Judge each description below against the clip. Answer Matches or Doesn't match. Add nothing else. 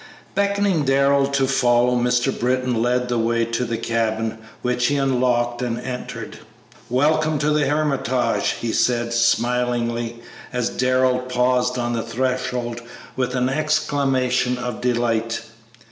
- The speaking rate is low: Matches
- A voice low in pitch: Matches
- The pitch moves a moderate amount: Doesn't match